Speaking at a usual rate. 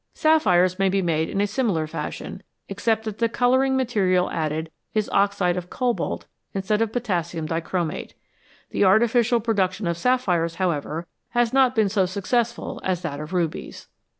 Yes: average, 160 wpm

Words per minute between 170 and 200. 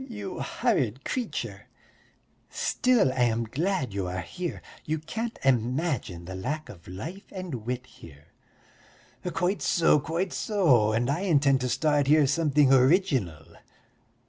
No: average, 140 wpm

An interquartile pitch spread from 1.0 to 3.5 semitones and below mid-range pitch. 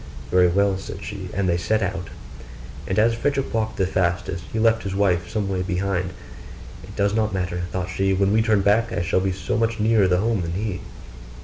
Yes: average, 2.9 semitones; very low, 95 Hz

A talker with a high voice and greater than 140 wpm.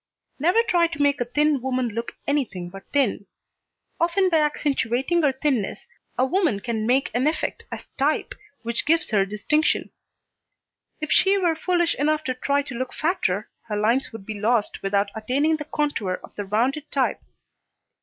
Yes: very high, 265 Hz; average, 170 wpm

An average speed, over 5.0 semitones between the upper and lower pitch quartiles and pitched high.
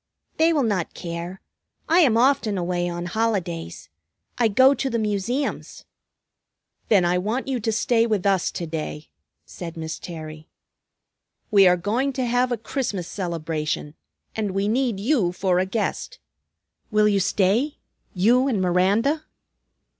Yes: average, 145 wpm; wide, 5.4 semitones; high, 205 Hz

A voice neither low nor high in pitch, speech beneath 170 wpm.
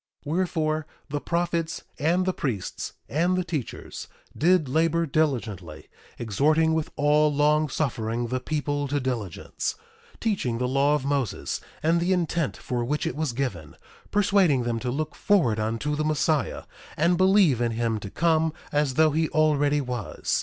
Yes: medium, 150 Hz; average, 160 wpm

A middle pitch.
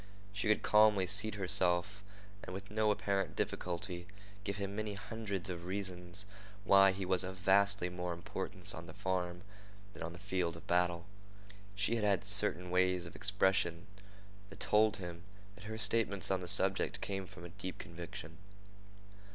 No: very low, 95 Hz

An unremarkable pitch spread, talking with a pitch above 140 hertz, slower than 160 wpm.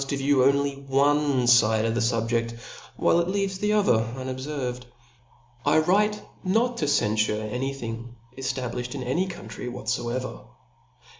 No: average, 4.0 semitones; low, 130 Hz; average, 140 wpm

